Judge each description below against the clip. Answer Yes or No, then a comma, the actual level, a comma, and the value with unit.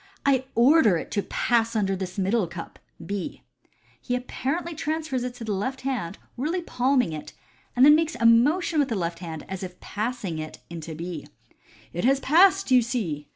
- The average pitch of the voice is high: Yes, high, 235 Hz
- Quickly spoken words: No, average, 195 wpm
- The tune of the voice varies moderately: No, wide, 6.9 semitones